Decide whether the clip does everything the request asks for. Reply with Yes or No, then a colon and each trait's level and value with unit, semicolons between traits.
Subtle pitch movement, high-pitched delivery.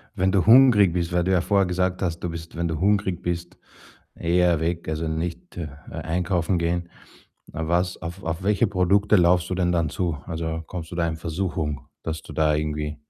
No: narrow, 2.0 semitones; very low, 85 Hz